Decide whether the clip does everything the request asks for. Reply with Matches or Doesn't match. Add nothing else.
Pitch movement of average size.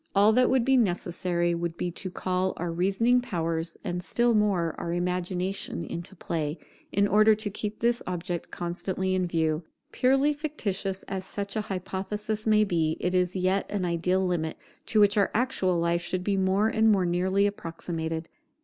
Matches